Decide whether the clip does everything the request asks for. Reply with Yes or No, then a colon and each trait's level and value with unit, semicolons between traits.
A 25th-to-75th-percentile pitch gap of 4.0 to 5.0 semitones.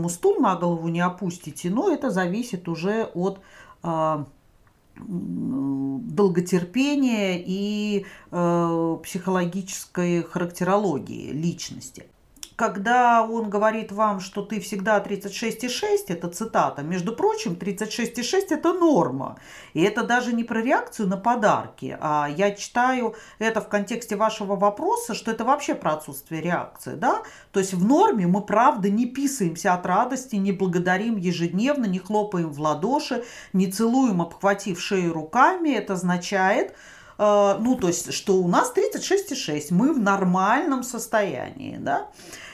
Yes: average, 4.7 semitones